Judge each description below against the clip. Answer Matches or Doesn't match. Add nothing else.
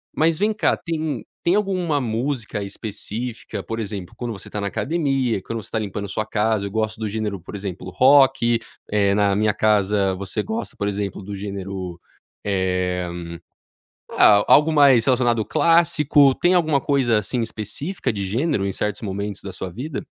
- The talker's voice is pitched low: Matches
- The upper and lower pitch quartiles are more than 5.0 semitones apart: Matches